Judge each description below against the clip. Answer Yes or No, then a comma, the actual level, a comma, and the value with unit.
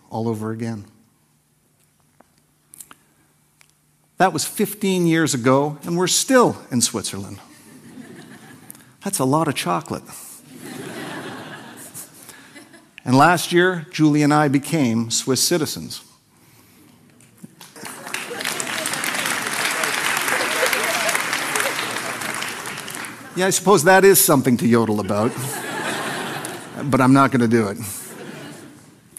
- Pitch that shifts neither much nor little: No, wide, 6.9 semitones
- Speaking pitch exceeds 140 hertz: No, low, 135 Hz